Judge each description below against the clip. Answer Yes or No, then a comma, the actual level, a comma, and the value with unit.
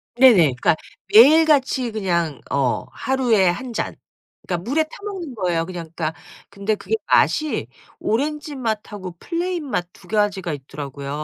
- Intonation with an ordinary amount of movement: No, wide, 8.1 semitones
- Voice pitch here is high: Yes, high, 215 Hz